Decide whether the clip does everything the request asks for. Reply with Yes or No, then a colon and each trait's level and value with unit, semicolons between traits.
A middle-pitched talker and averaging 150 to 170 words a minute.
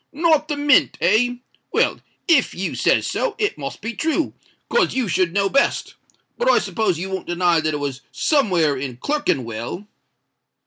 No: high, 200 Hz; average, 155 wpm